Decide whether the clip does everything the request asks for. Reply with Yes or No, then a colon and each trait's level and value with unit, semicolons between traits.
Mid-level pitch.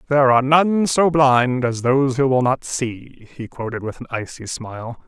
No: low, 130 Hz